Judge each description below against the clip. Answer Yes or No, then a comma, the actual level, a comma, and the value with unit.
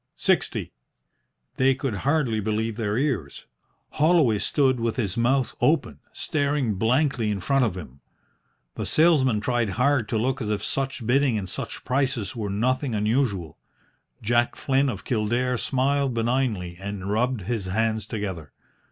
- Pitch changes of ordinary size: Yes, average, 4.2 semitones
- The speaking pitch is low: Yes, low, 120 Hz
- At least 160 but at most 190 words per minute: No, average, 145 wpm